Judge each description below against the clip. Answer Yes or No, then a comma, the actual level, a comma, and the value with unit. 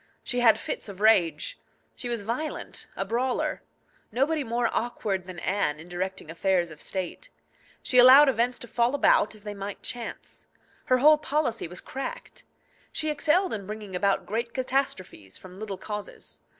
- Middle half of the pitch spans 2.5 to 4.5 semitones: No, average, 5.1 semitones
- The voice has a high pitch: Yes, high, 225 Hz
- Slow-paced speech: No, average, 165 wpm